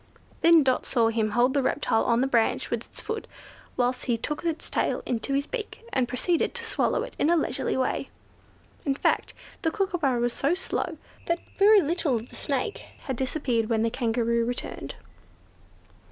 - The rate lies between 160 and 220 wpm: Yes, average, 180 wpm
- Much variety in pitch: Yes, wide, 6.0 semitones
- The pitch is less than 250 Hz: No, very high, 265 Hz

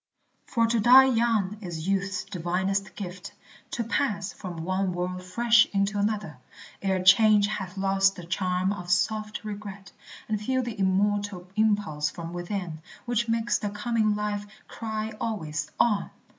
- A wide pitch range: No, average, 2.9 semitones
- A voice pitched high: Yes, high, 200 Hz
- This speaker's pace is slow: No, average, 145 wpm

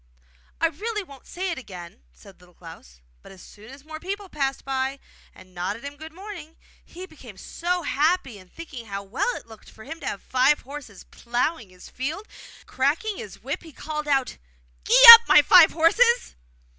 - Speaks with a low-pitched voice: No, very high, 280 Hz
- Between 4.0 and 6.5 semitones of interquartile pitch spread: No, wide, 7.4 semitones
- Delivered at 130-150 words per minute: No, average, 180 wpm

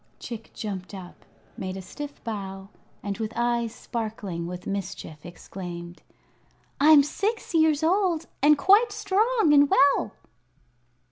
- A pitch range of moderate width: No, wide, 8.6 semitones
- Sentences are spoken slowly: Yes, slow, 125 wpm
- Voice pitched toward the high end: Yes, high, 230 Hz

